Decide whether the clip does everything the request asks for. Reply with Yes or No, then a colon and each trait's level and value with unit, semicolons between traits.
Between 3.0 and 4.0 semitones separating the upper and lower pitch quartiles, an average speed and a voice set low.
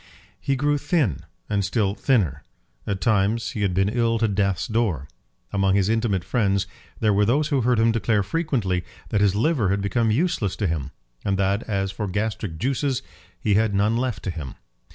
Yes: average, 3.3 semitones; average, 190 wpm; low, 105 Hz